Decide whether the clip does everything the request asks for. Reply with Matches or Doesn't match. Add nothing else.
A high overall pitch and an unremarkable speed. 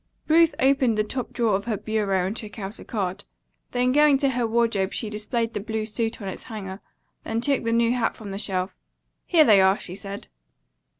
Doesn't match